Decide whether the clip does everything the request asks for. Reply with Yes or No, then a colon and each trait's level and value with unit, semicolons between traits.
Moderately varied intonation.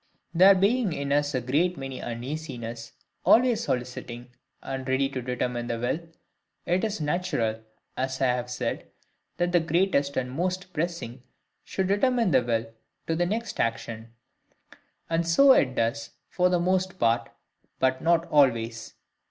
No: wide, 6.5 semitones